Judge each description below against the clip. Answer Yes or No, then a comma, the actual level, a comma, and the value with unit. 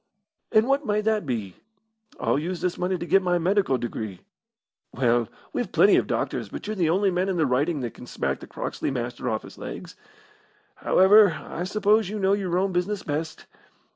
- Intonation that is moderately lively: No, wide, 6.9 semitones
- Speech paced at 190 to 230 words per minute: Yes, average, 195 wpm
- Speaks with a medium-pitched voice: Yes, medium, 180 Hz